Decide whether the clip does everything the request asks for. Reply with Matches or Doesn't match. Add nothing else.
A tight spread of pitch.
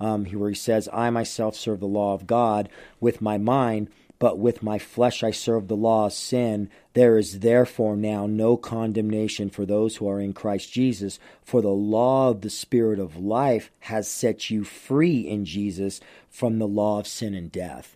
Matches